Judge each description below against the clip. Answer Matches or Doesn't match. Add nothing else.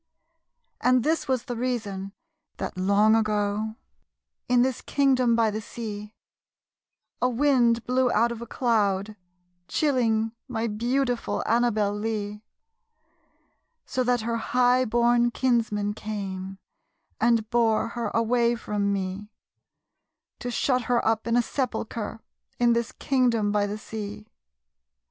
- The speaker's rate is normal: Doesn't match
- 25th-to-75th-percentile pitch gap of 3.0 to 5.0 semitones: Doesn't match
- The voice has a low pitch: Doesn't match